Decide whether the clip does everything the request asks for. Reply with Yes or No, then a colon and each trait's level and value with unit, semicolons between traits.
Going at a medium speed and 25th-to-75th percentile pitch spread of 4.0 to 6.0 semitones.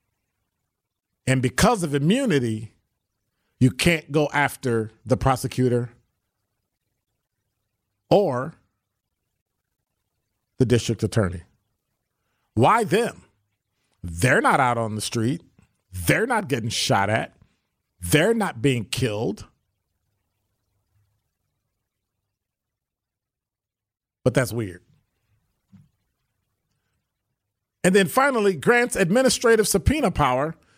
No: slow, 80 wpm; average, 4.5 semitones